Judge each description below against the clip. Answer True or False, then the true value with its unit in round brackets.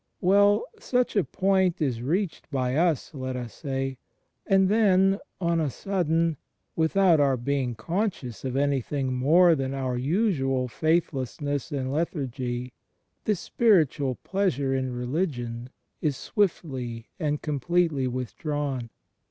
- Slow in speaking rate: True (120 wpm)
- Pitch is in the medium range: True (145 Hz)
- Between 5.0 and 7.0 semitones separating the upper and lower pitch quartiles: True (5.5 semitones)